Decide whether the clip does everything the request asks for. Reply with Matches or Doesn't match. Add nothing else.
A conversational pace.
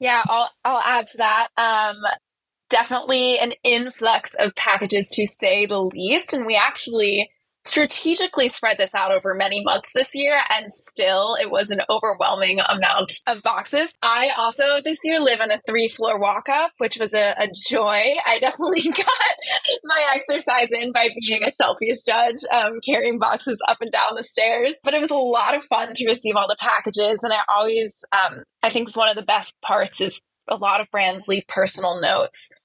Matches